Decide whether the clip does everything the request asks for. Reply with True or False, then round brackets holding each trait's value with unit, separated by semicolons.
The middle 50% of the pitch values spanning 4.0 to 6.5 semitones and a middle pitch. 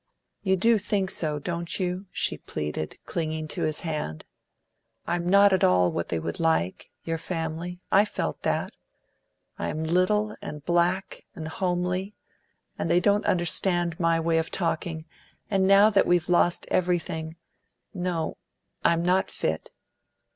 False (2.7 semitones; 175 Hz)